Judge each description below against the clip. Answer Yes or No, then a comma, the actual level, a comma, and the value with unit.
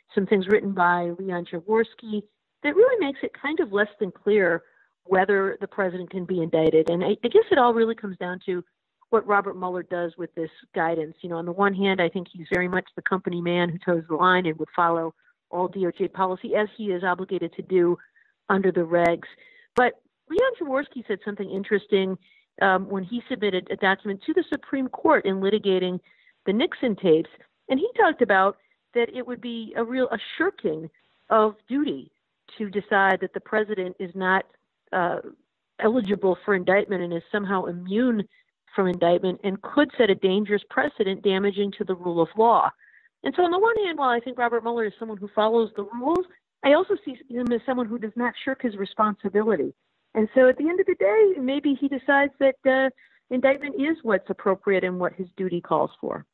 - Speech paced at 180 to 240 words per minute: Yes, average, 200 wpm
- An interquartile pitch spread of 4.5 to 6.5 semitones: Yes, average, 5.2 semitones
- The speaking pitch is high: Yes, high, 205 Hz